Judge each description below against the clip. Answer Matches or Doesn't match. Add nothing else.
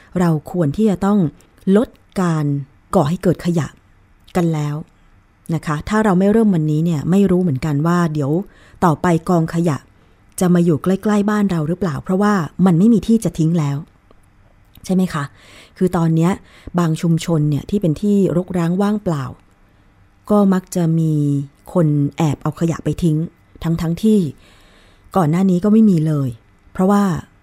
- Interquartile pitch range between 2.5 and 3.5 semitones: Doesn't match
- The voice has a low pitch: Doesn't match